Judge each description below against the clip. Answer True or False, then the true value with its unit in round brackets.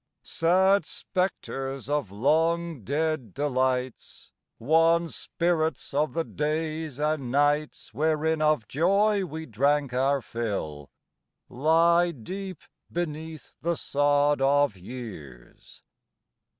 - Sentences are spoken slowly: True (100 wpm)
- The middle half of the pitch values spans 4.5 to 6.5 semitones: False (3.8 semitones)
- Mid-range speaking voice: True (150 Hz)